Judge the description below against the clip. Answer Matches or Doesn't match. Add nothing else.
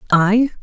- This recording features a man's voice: Doesn't match